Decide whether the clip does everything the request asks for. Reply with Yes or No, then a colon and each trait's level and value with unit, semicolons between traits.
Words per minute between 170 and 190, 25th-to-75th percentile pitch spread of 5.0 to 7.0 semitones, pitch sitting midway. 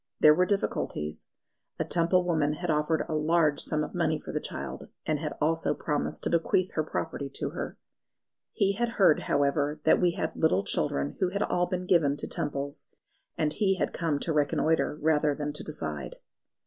No: average, 185 wpm; average, 3.2 semitones; medium, 155 Hz